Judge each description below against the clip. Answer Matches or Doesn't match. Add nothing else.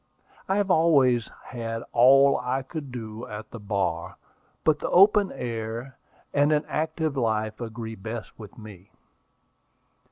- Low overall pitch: Matches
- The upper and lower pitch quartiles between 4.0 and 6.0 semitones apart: Matches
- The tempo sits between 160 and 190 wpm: Doesn't match